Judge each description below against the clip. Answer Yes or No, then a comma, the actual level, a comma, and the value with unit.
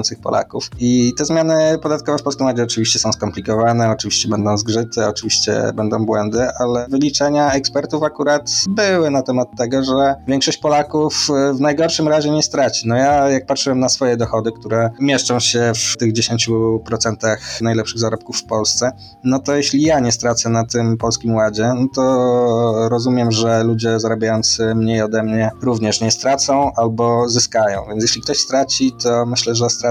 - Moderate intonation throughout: Yes, average, 3.3 semitones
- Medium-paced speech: No, fast, 165 wpm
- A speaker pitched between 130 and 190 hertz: No, low, 120 Hz